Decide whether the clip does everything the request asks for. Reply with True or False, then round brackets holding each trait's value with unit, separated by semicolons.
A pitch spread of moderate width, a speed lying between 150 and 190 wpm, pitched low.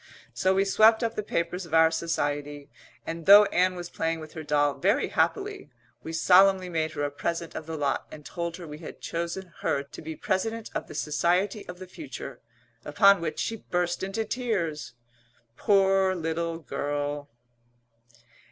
False (3.6 semitones; 170 wpm; 170 Hz)